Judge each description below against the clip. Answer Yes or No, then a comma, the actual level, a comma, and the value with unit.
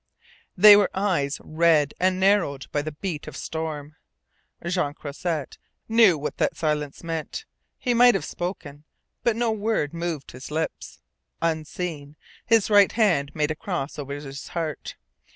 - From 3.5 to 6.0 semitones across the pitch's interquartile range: Yes, average, 4.9 semitones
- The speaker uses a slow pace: No, average, 150 wpm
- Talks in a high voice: No, medium, 160 Hz